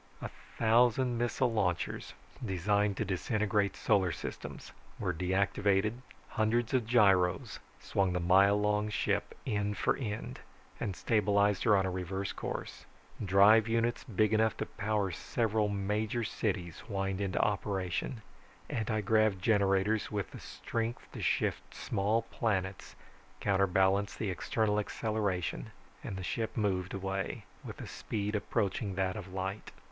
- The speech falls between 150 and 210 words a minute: No, slow, 135 wpm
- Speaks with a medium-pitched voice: No, low, 100 Hz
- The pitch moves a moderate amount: No, narrow, 2.3 semitones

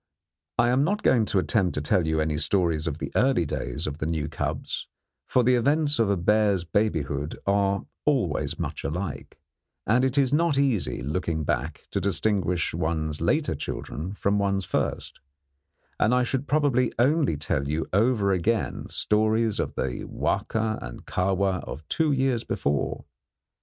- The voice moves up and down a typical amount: No, wide, 7.2 semitones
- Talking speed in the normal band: Yes, average, 160 wpm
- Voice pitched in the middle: No, low, 100 Hz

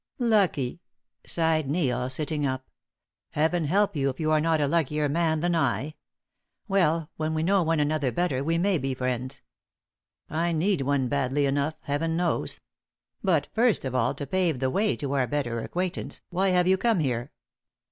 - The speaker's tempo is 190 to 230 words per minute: No, average, 175 wpm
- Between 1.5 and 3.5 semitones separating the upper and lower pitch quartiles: No, average, 4.1 semitones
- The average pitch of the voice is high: No, medium, 155 Hz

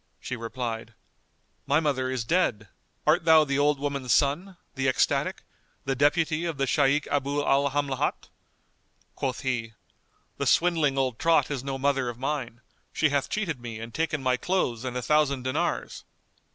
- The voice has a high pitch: No, low, 135 Hz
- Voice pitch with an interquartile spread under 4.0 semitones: Yes, average, 2.7 semitones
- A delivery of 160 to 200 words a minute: Yes, average, 165 wpm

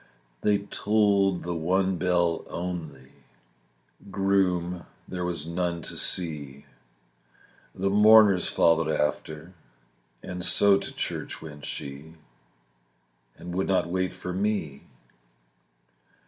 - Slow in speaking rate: Yes, slow, 105 wpm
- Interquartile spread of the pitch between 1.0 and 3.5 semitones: Yes, average, 2.9 semitones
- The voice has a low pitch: Yes, very low, 90 Hz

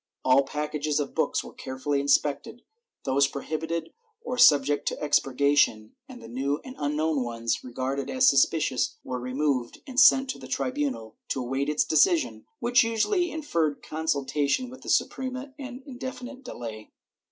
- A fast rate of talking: No, average, 155 wpm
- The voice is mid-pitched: Yes, medium, 150 Hz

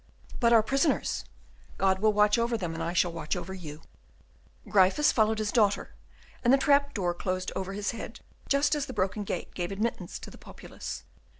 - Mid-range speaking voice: No, high, 210 Hz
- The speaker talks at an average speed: Yes, average, 190 wpm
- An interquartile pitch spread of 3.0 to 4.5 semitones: Yes, average, 4.2 semitones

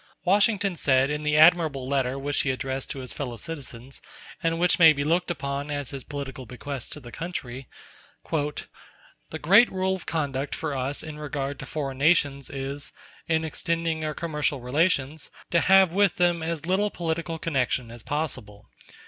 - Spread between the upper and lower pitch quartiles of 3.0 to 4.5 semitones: Yes, average, 3.6 semitones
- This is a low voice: No, medium, 150 Hz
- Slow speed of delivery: No, average, 170 wpm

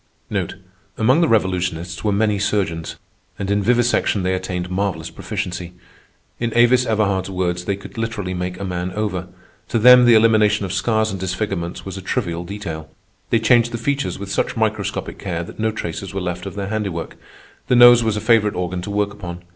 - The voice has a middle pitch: No, low, 100 Hz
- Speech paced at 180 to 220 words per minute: Yes, average, 185 wpm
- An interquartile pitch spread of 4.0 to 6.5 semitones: No, average, 3.5 semitones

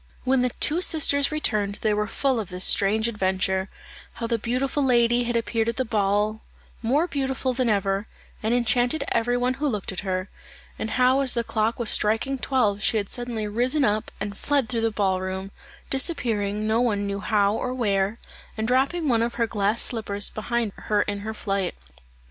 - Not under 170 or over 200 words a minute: Yes, average, 190 wpm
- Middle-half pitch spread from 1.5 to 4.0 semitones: Yes, average, 3.6 semitones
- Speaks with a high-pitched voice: Yes, high, 225 Hz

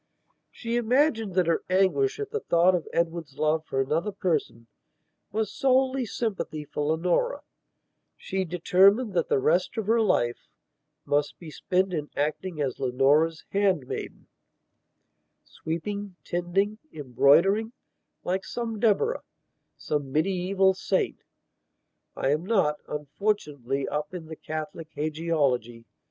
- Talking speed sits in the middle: No, slow, 115 wpm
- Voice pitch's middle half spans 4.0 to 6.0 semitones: Yes, average, 5.2 semitones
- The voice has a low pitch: No, medium, 175 Hz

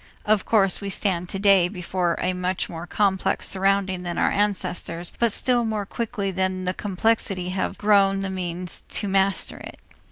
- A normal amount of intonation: No, narrow, 1.9 semitones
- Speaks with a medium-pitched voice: No, high, 195 Hz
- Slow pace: No, average, 165 wpm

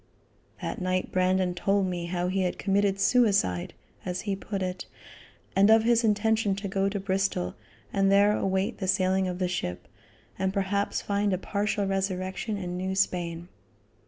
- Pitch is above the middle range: Yes, high, 195 Hz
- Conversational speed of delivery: Yes, average, 170 wpm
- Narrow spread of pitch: Yes, narrow, 1.6 semitones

